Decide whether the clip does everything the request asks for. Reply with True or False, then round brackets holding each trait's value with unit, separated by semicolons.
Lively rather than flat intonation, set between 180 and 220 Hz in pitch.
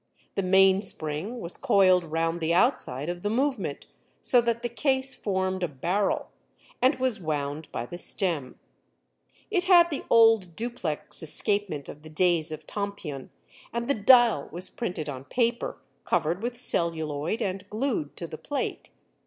True (6.8 semitones; 185 Hz)